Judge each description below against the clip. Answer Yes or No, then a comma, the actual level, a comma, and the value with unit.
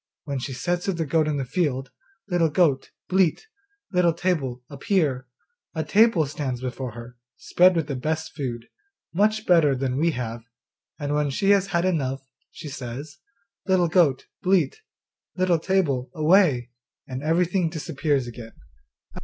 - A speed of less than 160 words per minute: Yes, average, 150 wpm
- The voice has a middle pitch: Yes, medium, 155 Hz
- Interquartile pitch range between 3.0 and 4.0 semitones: No, average, 5.1 semitones